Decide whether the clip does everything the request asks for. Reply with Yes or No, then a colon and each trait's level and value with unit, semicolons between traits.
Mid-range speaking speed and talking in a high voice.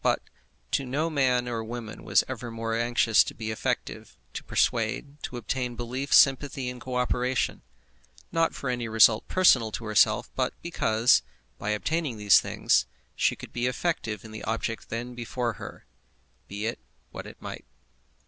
No: average, 160 wpm; low, 120 Hz